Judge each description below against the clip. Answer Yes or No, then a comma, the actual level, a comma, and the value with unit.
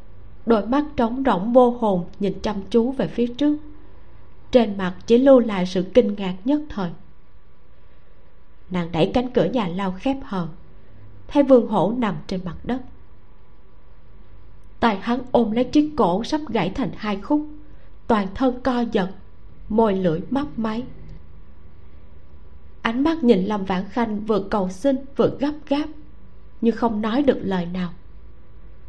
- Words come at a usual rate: No, slow, 155 wpm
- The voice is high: Yes, high, 220 Hz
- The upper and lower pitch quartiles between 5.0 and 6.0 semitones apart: Yes, wide, 5.6 semitones